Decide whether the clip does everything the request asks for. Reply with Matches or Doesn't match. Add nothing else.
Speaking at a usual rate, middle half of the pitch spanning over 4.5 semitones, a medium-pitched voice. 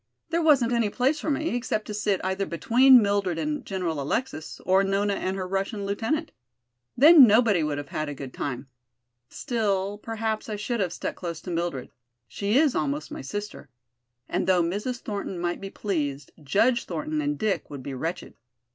Doesn't match